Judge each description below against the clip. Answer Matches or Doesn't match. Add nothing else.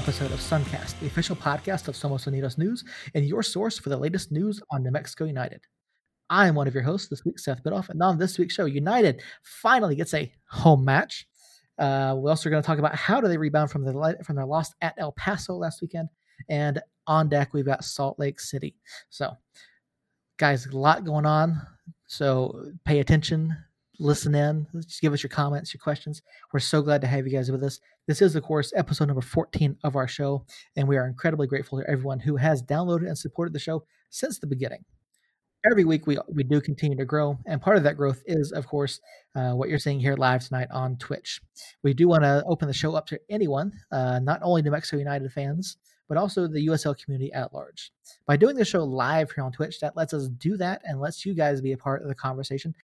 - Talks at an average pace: Doesn't match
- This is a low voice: Doesn't match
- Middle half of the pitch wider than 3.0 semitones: Doesn't match